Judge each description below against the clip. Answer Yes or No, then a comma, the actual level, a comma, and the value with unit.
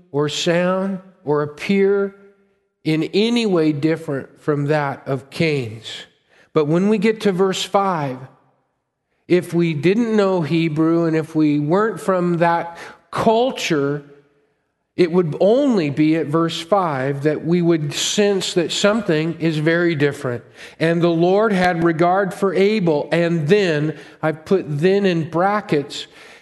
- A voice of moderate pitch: Yes, medium, 170 Hz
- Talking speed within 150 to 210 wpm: No, average, 140 wpm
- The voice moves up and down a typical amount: Yes, average, 4.2 semitones